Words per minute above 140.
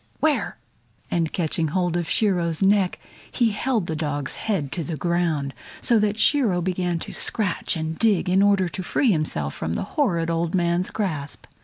Yes: average, 175 wpm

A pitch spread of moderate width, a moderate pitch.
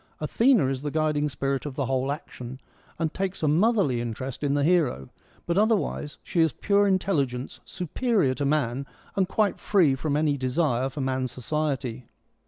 Yes: average, 4.9 semitones; medium, 145 Hz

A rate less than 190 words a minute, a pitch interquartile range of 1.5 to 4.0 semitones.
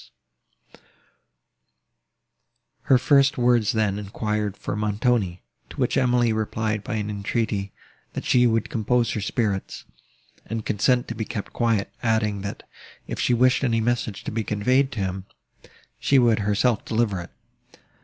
Yes: average, 145 wpm; average, 2.8 semitones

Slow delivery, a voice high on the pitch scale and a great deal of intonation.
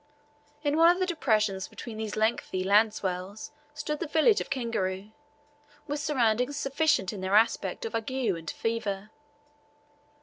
No: average, 145 wpm; high, 225 Hz; wide, 6.4 semitones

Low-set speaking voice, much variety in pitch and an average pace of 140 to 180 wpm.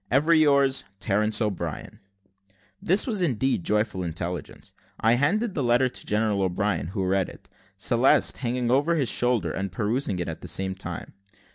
Yes: low, 115 Hz; wide, 5.8 semitones; average, 160 wpm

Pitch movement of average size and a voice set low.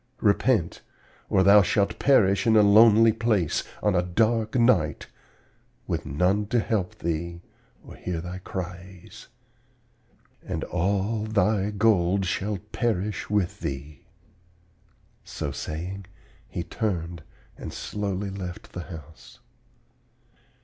Yes: average, 3.3 semitones; very low, 95 Hz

